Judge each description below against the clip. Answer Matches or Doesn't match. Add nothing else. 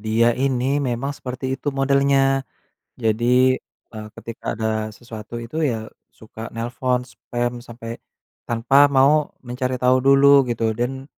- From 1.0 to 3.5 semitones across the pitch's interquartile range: Matches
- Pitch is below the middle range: Matches